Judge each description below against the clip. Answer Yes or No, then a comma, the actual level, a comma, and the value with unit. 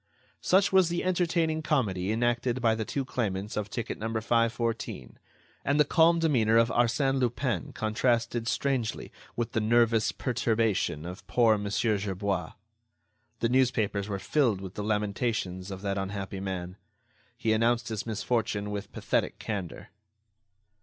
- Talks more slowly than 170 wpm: Yes, average, 140 wpm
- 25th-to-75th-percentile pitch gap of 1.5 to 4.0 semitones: Yes, average, 3.3 semitones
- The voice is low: Yes, low, 115 Hz